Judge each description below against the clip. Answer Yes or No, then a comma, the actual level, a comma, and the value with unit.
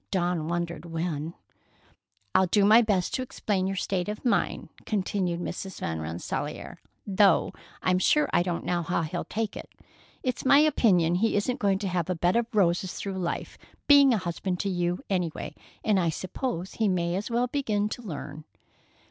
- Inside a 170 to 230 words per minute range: Yes, average, 180 wpm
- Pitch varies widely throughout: No, average, 3.5 semitones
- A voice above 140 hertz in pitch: Yes, medium, 185 Hz